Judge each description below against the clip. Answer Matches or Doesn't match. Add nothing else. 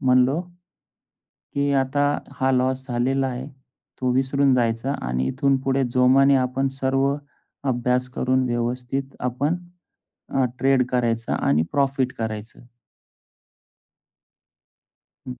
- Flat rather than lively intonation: Matches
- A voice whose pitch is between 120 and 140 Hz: Matches